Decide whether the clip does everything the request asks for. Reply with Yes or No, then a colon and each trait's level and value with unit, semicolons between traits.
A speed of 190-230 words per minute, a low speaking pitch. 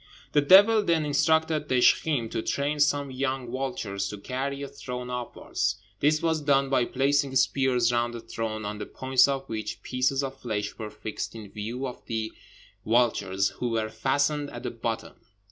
No: average, 175 wpm; low, 130 Hz